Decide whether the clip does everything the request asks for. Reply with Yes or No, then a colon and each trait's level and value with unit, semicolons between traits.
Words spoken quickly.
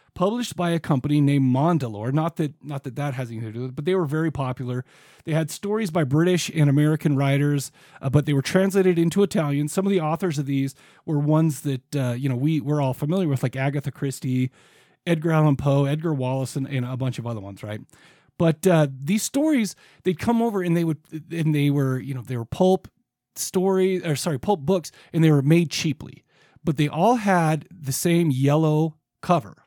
Yes: fast, 215 wpm